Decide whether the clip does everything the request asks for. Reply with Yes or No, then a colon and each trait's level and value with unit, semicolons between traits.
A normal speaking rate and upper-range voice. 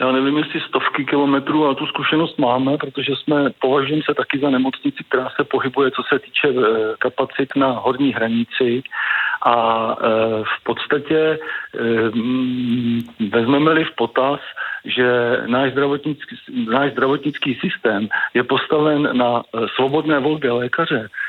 No: average, 125 wpm; medium, 140 Hz